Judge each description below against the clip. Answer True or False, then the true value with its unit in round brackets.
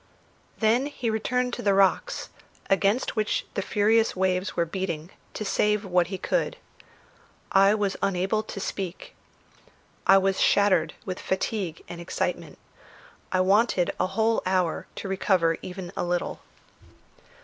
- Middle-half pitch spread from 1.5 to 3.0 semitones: True (2.5 semitones)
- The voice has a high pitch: True (195 Hz)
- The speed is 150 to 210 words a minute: False (140 wpm)